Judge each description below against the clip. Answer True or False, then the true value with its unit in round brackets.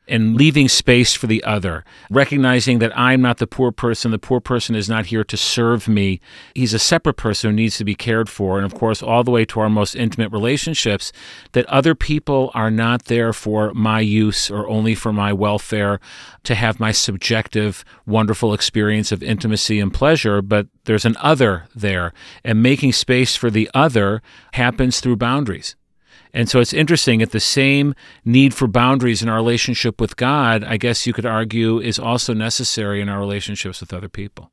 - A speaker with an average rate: True (190 wpm)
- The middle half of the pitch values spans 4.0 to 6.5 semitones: False (2.7 semitones)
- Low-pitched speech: True (115 Hz)